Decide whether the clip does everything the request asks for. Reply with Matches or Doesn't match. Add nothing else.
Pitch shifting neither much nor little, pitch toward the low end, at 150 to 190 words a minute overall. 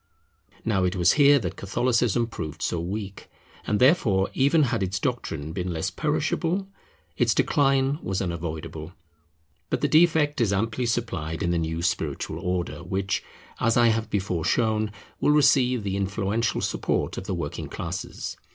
Doesn't match